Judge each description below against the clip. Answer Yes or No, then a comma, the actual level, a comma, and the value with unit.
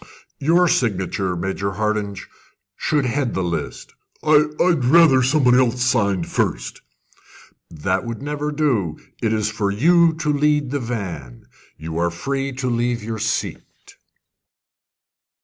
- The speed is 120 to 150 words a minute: Yes, slow, 135 wpm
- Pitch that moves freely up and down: Yes, wide, 6.6 semitones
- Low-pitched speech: Yes, low, 120 Hz